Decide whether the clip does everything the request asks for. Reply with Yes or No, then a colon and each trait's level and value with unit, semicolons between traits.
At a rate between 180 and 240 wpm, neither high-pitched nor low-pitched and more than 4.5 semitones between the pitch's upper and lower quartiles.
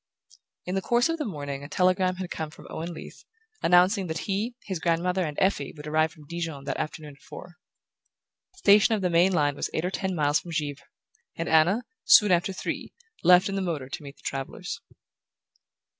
No: fast, 205 wpm; medium, 175 Hz; average, 3.8 semitones